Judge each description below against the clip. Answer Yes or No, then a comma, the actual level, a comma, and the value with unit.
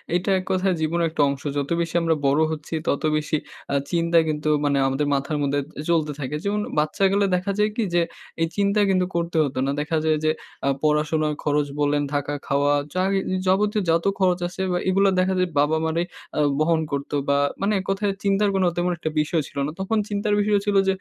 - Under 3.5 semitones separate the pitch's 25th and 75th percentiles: No, average, 4.3 semitones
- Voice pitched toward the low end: No, medium, 165 Hz